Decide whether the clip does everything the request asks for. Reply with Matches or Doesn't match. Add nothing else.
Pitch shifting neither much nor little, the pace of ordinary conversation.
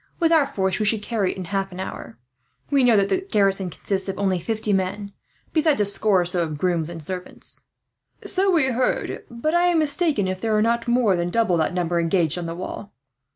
Doesn't match